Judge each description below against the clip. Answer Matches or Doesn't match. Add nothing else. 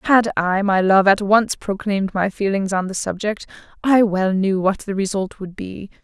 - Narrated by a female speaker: Matches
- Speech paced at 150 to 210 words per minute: Matches